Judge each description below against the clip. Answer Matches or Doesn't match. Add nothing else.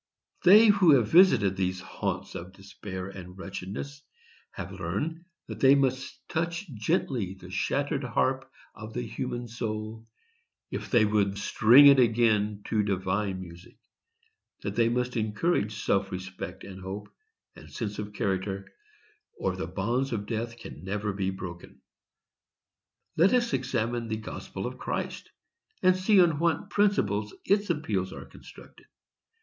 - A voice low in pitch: Matches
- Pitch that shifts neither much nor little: Doesn't match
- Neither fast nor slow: Matches